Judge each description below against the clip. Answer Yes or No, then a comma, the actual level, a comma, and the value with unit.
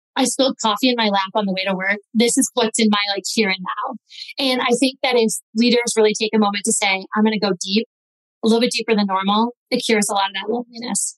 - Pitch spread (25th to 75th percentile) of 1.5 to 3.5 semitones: Yes, average, 3.0 semitones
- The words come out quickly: Yes, fast, 270 wpm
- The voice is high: Yes, high, 225 Hz